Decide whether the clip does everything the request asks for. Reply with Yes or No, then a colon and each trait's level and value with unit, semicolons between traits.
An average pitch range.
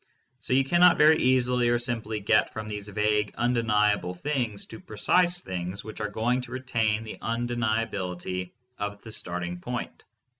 Yes: average, 3.1 semitones